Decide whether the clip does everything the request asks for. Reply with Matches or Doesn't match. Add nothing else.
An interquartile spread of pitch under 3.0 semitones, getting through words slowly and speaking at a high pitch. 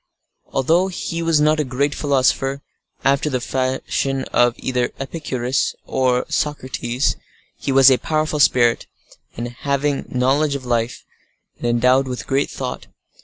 Doesn't match